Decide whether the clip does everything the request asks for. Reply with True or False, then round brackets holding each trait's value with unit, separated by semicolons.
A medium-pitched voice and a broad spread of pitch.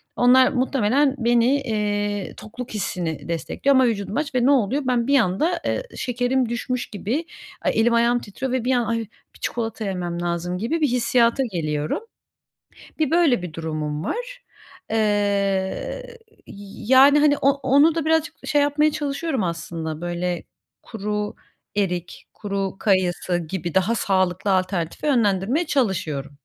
False (225 Hz; 6.2 semitones)